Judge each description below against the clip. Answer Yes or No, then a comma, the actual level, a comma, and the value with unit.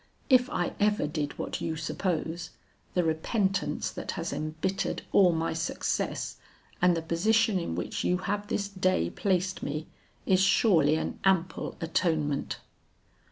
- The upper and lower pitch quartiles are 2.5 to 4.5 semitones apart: Yes, average, 3.4 semitones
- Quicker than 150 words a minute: No, average, 140 wpm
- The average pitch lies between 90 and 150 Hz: No, medium, 175 Hz